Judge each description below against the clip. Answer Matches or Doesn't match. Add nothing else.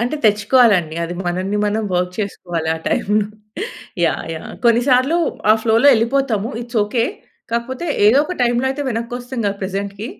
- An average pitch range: Matches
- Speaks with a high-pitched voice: Matches